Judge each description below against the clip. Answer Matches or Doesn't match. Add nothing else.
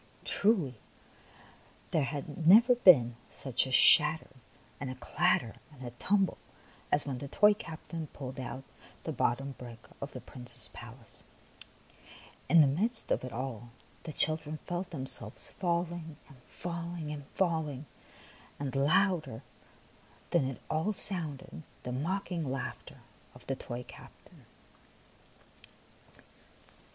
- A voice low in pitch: Doesn't match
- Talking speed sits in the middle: Doesn't match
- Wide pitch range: Doesn't match